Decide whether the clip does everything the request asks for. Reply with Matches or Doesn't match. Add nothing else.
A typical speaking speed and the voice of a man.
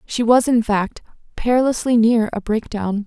Doesn't match